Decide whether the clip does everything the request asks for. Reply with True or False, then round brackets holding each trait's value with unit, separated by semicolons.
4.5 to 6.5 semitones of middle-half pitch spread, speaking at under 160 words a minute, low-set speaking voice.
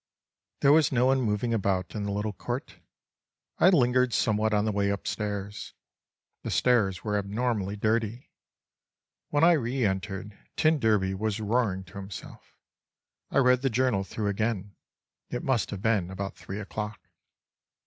False (3.6 semitones; 150 wpm; 105 Hz)